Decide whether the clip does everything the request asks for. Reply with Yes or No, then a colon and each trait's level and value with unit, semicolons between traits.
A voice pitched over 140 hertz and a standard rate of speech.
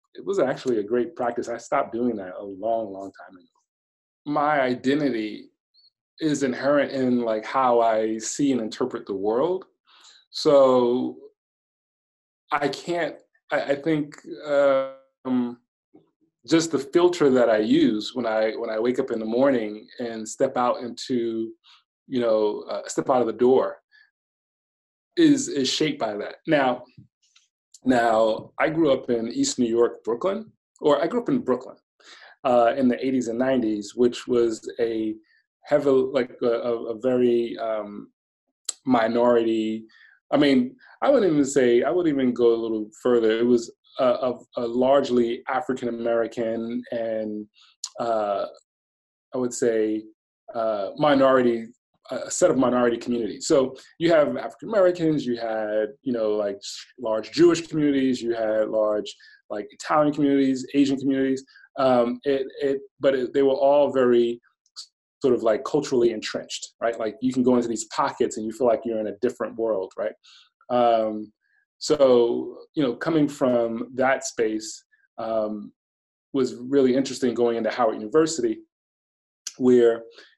No: low, 120 Hz; average, 150 wpm